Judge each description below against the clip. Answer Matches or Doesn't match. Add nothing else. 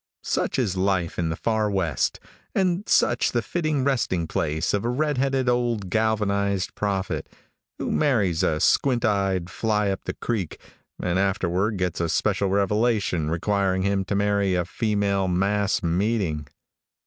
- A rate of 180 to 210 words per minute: Doesn't match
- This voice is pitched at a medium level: Doesn't match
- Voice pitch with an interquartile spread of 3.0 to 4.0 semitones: Matches